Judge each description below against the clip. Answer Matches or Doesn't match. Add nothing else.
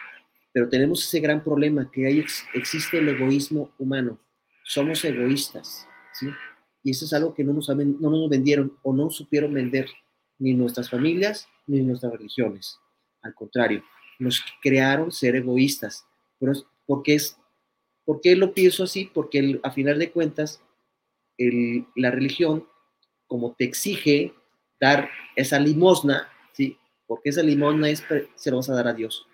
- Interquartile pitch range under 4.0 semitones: Matches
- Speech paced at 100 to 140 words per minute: Doesn't match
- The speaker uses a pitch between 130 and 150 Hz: Matches